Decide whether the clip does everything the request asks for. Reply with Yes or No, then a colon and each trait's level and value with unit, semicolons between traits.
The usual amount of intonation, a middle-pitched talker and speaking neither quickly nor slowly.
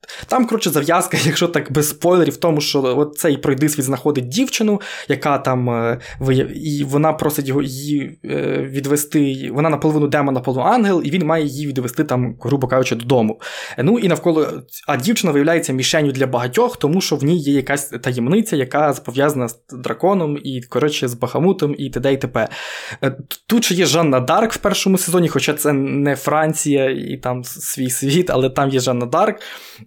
No: average, 3.8 semitones; medium, 145 Hz; fast, 180 wpm